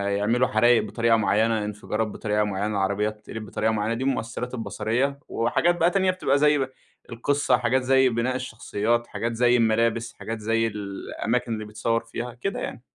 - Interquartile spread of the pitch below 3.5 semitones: Yes, average, 2.7 semitones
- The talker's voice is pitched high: No, low, 115 Hz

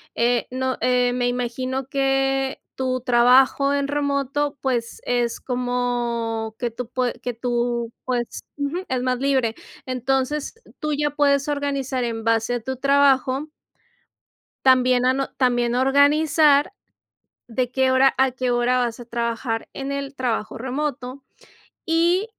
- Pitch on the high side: Yes, very high, 255 Hz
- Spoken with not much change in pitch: Yes, narrow, 2.3 semitones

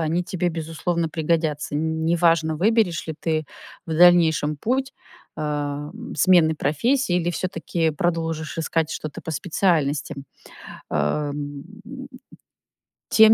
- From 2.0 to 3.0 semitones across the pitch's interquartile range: Yes, narrow, 2.5 semitones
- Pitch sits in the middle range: Yes, medium, 160 Hz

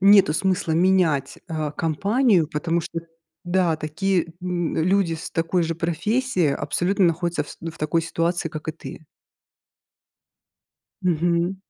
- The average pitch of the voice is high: No, medium, 170 Hz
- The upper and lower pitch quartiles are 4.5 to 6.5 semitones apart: No, narrow, 2.6 semitones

